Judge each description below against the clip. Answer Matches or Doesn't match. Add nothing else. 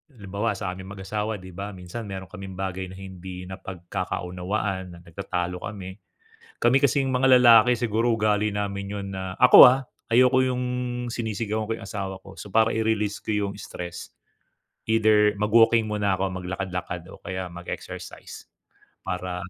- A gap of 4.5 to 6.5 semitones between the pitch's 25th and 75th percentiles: Doesn't match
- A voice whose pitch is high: Doesn't match